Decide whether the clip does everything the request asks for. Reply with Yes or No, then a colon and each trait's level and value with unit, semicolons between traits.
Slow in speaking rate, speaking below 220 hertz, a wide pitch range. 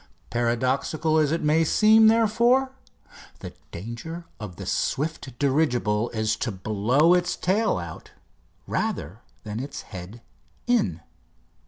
Yes: slow, 120 wpm; low, 135 Hz; wide, 7.4 semitones